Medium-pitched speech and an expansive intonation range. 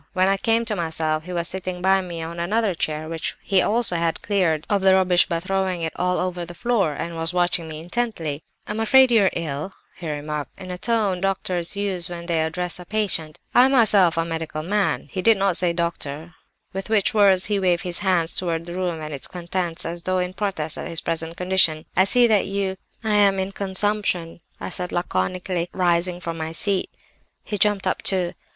No: medium, 180 Hz; average, 2.8 semitones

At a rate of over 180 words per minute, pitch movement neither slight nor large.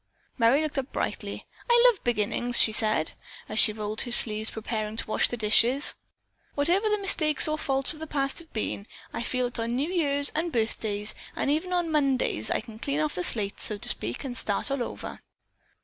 No: fast, 205 wpm; wide, 5.8 semitones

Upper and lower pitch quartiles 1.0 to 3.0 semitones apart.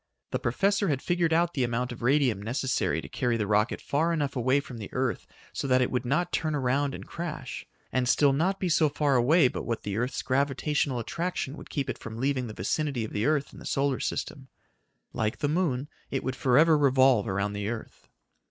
No: average, 3.6 semitones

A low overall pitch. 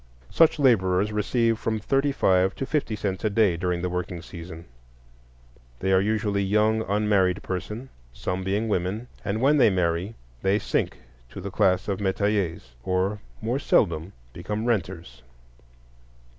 Yes: low, 100 Hz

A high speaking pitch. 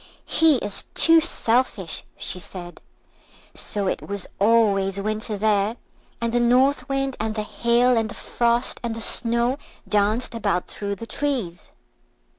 Yes: high, 225 Hz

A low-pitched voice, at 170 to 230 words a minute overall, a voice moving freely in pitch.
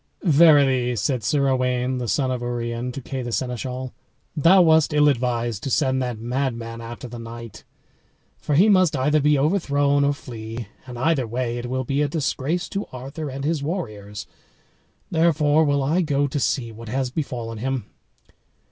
No: low, 130 Hz; average, 175 wpm; average, 3.4 semitones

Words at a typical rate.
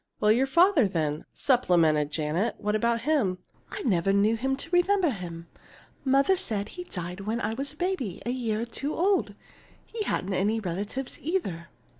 Yes: average, 175 wpm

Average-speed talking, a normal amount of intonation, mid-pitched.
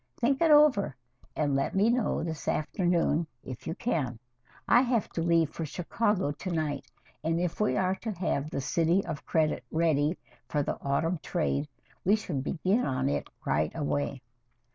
Yes: average, 175 wpm; average, 4.9 semitones; medium, 165 Hz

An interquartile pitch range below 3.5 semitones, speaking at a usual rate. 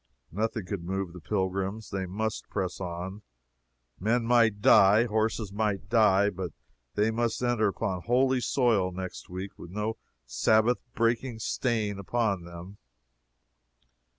No: average, 3.1 semitones; slow, 130 wpm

